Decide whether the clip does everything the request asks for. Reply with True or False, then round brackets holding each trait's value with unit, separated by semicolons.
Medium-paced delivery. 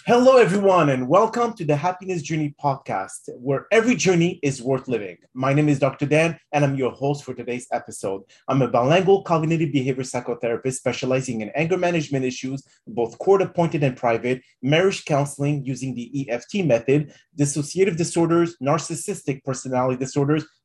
True (155 wpm)